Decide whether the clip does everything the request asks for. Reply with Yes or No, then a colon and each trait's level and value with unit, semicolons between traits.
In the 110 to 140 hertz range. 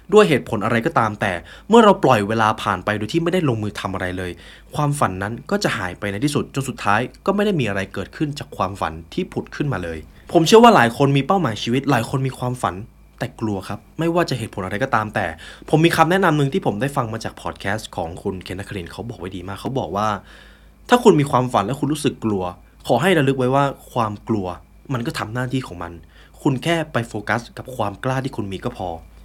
Yes: low, 115 Hz